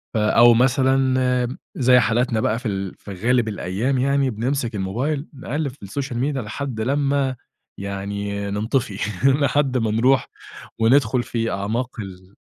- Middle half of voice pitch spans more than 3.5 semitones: Yes, average, 4.1 semitones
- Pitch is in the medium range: No, low, 120 Hz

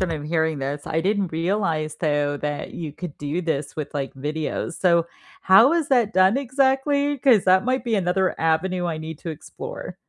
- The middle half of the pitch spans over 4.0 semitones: Yes, average, 5.3 semitones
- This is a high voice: No, medium, 170 Hz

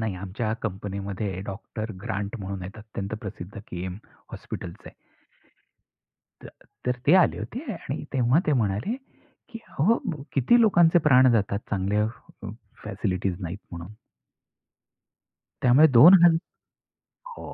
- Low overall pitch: Yes, low, 105 Hz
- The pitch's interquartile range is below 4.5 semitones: No, wide, 5.6 semitones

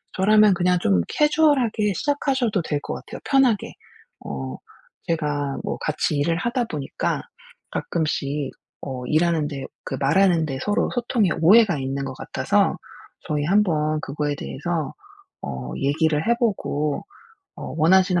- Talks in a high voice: No, medium, 160 Hz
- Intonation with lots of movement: Yes, wide, 6.3 semitones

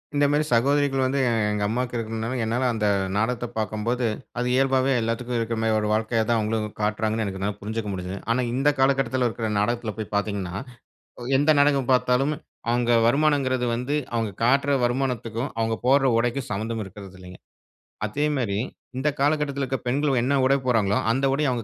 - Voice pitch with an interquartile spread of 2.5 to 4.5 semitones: Yes, average, 3.5 semitones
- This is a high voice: No, low, 120 Hz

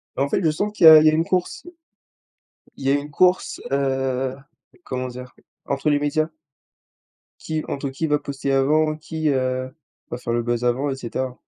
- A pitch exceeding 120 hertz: Yes, medium, 140 Hz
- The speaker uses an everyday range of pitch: Yes, average, 3.1 semitones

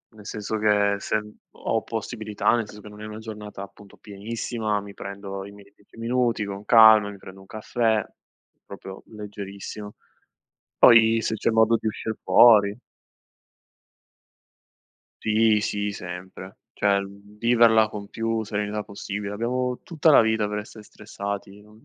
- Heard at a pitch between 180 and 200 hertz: No, low, 105 Hz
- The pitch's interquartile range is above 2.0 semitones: No, narrow, 1.6 semitones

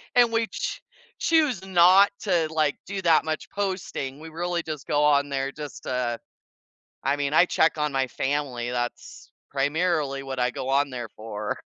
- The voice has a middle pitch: Yes, medium, 150 Hz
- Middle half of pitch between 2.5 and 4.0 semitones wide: No, average, 4.5 semitones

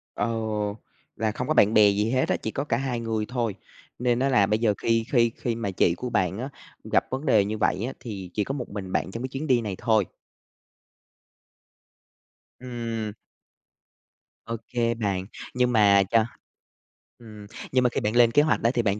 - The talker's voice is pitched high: No, low, 115 Hz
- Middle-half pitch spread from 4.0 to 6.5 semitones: No, average, 2.9 semitones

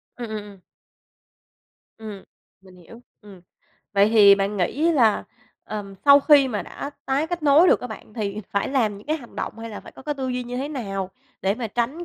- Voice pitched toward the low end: No, high, 230 Hz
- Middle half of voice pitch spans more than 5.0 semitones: Yes, wide, 5.4 semitones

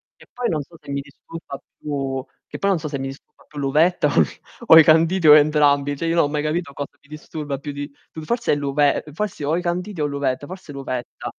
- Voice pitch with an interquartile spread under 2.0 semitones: No, average, 2.7 semitones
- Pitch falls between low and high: Yes, medium, 150 Hz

